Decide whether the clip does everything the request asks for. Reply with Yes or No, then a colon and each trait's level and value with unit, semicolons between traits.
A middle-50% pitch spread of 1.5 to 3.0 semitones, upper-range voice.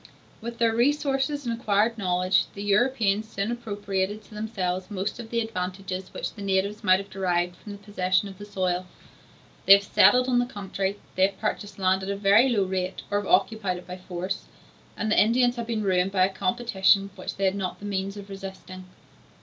Yes: average, 2.7 semitones; high, 200 Hz